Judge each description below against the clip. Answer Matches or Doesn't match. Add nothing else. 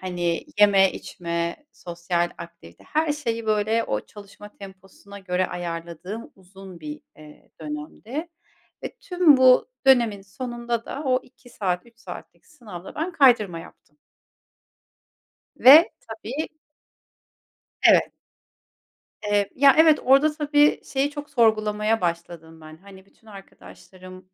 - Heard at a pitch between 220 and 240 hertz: Doesn't match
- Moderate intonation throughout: Doesn't match